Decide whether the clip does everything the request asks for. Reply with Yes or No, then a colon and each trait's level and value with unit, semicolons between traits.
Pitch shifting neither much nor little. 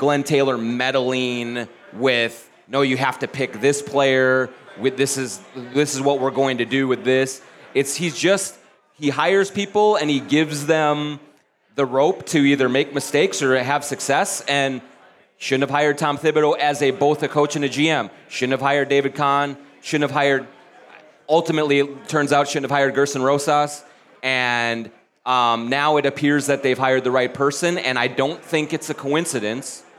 No: narrow, 2.0 semitones